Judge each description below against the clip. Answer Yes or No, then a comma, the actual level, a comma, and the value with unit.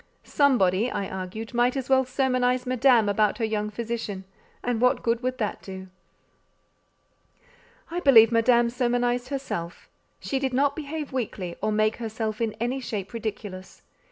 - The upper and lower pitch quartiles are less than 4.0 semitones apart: Yes, average, 3.1 semitones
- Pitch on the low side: No, high, 235 Hz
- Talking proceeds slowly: No, average, 150 wpm